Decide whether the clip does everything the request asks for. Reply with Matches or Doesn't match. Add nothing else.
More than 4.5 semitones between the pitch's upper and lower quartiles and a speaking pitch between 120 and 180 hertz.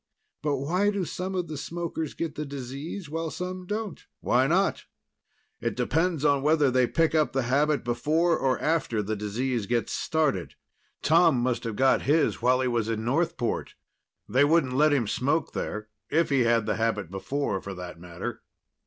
Matches